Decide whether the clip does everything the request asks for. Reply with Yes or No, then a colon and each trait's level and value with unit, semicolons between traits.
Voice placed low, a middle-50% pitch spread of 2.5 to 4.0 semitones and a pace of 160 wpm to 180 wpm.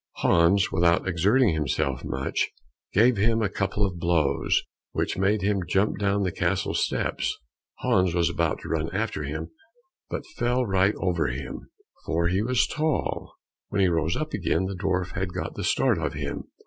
Yes: very low, 95 Hz; average, 3.4 semitones; average, 175 wpm